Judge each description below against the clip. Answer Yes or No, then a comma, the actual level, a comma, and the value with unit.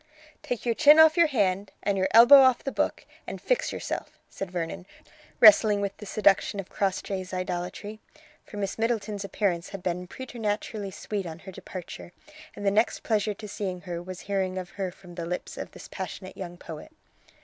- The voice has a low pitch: No, high, 195 Hz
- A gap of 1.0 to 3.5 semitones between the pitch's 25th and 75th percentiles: Yes, average, 2.8 semitones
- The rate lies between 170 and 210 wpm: Yes, average, 185 wpm